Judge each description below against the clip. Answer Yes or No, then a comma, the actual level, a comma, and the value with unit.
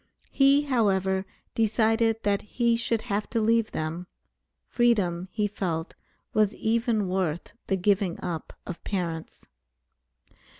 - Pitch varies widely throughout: No, average, 3.8 semitones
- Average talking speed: No, slow, 120 wpm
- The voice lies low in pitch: No, high, 205 Hz